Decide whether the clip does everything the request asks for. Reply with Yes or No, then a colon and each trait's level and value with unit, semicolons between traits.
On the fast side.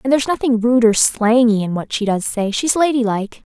Yes: fast, 220 wpm